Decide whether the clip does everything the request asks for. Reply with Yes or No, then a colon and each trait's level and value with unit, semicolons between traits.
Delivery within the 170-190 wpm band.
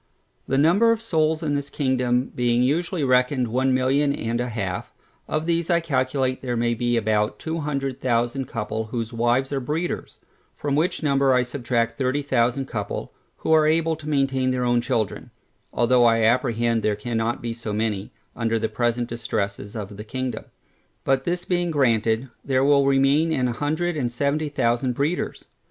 Yes: average, 175 wpm